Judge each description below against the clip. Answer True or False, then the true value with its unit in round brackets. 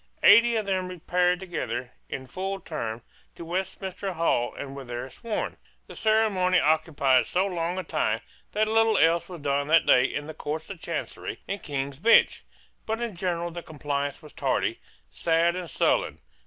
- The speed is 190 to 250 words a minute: False (170 wpm)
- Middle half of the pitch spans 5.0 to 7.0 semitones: False (4.6 semitones)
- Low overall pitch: False (170 Hz)